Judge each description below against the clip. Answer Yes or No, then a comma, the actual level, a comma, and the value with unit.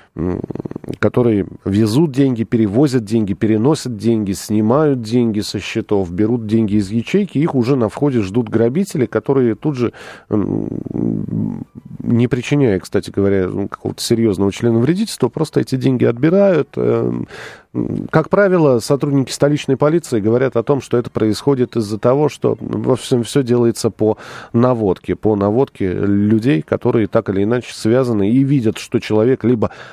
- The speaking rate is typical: Yes, average, 135 wpm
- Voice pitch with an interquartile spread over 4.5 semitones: No, average, 4.1 semitones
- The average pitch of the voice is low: Yes, low, 120 Hz